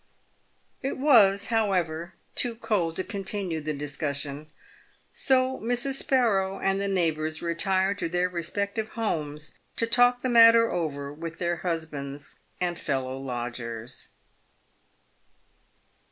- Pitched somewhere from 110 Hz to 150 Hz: No, medium, 175 Hz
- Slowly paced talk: Yes, slow, 115 wpm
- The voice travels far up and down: Yes, wide, 6.3 semitones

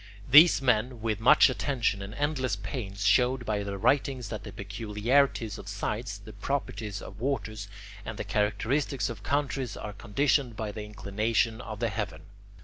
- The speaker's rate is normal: Yes, average, 160 wpm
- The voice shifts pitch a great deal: No, average, 3.9 semitones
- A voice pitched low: Yes, low, 110 Hz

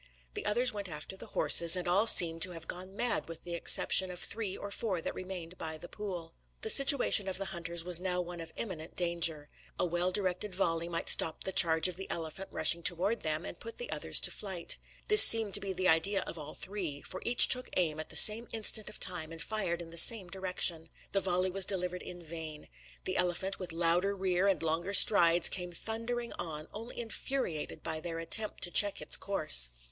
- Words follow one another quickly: Yes, fast, 215 wpm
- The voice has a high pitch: No, medium, 180 Hz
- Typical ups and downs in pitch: Yes, average, 3.2 semitones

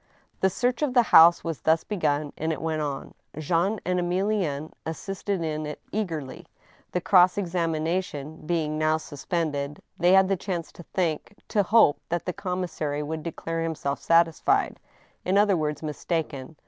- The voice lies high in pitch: No, medium, 165 Hz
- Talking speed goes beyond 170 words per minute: No, average, 165 wpm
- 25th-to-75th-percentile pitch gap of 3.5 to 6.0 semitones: No, average, 3.1 semitones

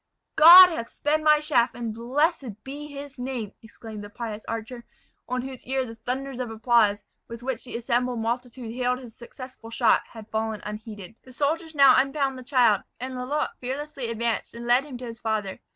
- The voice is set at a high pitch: Yes, high, 245 Hz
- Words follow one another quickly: No, average, 185 wpm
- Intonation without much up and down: No, average, 3.0 semitones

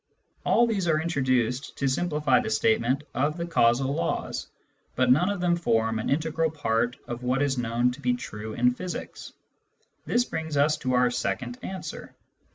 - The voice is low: Yes, low, 130 Hz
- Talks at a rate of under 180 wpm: Yes, average, 170 wpm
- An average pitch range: Yes, average, 4.8 semitones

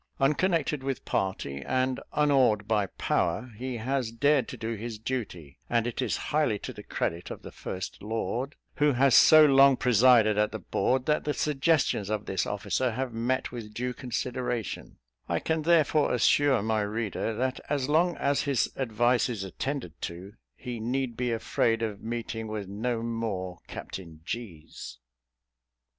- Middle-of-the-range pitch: No, low, 120 Hz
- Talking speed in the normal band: Yes, average, 165 wpm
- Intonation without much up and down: No, average, 3.9 semitones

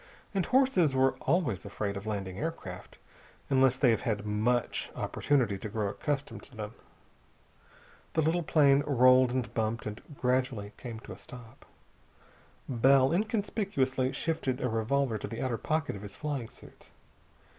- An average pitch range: Yes, average, 4.6 semitones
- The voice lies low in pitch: Yes, low, 130 Hz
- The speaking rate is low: No, average, 150 wpm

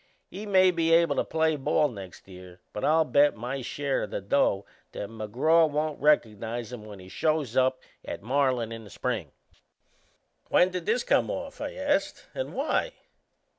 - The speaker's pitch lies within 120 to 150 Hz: Yes, medium, 140 Hz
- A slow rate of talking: No, average, 175 wpm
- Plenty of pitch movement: Yes, wide, 6.7 semitones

